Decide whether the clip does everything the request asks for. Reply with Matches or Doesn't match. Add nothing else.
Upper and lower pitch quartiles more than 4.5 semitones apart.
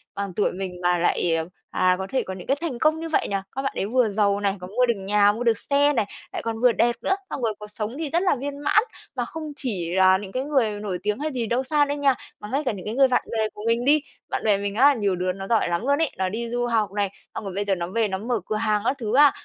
Matches